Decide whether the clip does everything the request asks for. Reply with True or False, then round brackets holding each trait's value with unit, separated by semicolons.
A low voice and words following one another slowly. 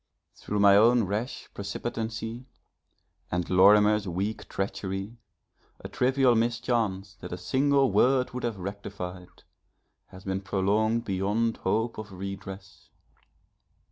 True (105 Hz; 110 wpm)